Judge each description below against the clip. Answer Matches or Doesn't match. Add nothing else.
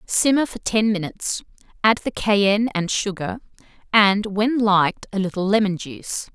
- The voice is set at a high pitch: Matches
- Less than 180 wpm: Matches